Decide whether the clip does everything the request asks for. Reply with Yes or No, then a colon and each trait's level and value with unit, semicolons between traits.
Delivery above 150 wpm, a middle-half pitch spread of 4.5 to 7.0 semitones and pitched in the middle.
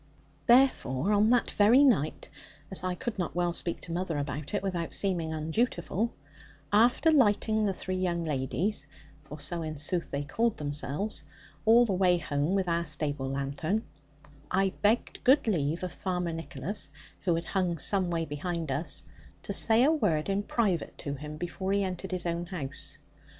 Yes: average, 170 wpm; average, 4.8 semitones; medium, 175 Hz